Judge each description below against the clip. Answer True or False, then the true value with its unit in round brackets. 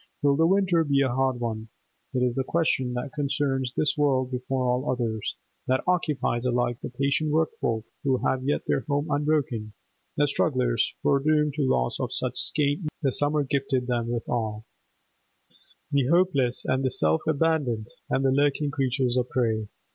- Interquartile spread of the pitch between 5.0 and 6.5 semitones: False (3.0 semitones)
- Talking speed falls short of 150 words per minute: False (170 wpm)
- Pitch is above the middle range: False (135 Hz)